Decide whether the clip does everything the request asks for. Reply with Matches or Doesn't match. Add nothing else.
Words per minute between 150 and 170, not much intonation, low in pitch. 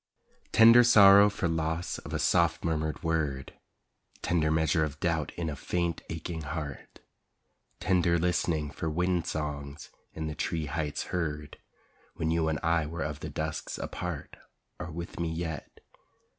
Matches